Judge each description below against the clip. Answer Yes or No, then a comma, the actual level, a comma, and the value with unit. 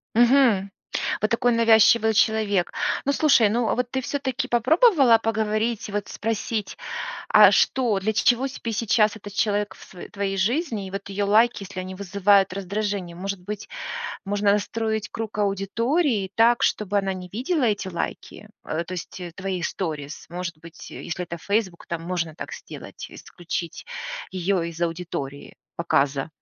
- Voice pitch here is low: No, high, 205 Hz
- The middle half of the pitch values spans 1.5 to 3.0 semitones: No, average, 3.6 semitones